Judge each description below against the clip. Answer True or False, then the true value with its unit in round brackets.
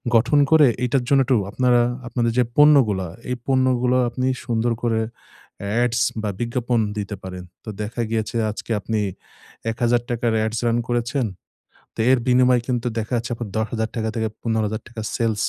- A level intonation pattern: True (2.1 semitones)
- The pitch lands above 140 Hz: False (120 Hz)